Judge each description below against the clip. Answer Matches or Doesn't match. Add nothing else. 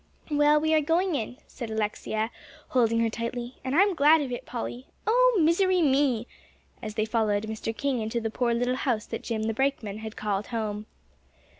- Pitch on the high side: Matches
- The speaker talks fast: Doesn't match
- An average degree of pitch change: Matches